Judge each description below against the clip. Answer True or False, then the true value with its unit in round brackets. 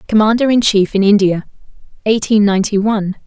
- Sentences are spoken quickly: False (145 wpm)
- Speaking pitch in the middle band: False (205 Hz)